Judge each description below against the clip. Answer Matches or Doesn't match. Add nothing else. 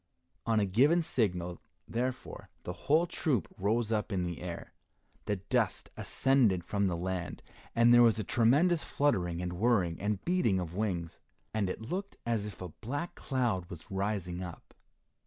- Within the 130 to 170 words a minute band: Matches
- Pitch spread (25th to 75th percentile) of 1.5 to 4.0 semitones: Doesn't match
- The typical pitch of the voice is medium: Doesn't match